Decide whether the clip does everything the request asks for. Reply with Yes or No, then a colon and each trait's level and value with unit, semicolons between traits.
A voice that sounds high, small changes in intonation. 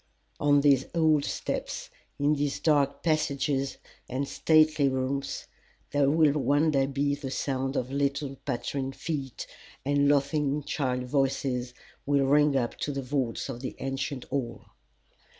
No: medium, 140 Hz; narrow, 1.4 semitones